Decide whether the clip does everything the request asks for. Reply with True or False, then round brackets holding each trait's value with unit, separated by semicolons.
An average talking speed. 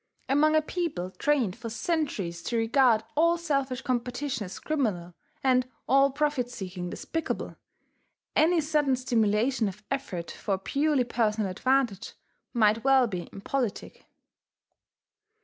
False (120 wpm)